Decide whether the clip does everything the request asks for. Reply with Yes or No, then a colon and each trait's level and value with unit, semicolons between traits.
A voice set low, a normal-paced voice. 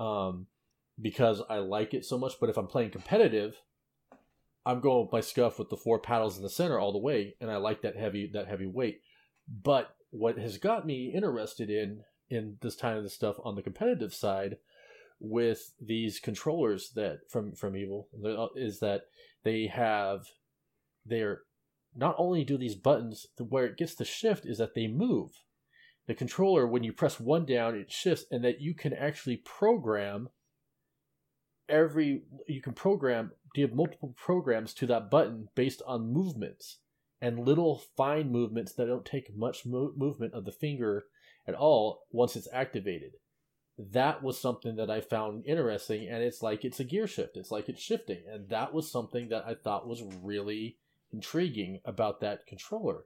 Yes: low, 120 Hz; average, 175 wpm